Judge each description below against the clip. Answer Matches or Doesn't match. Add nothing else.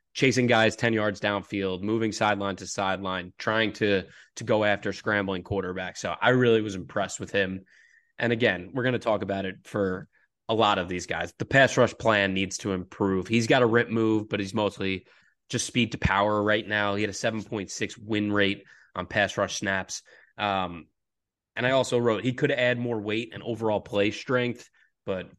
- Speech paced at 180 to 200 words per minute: Matches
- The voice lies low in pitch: Matches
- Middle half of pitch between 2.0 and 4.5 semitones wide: Matches